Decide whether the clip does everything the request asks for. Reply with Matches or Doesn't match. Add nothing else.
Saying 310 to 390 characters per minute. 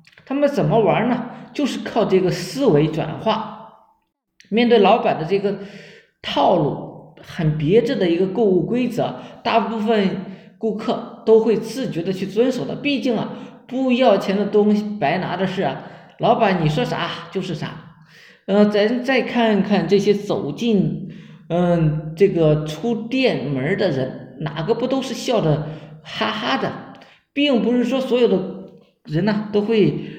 Doesn't match